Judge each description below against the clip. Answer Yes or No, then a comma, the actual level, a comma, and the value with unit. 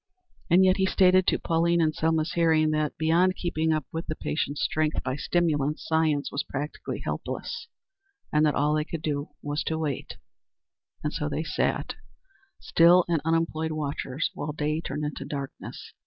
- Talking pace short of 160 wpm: No, average, 165 wpm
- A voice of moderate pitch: Yes, medium, 155 Hz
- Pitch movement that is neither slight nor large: No, narrow, 1.9 semitones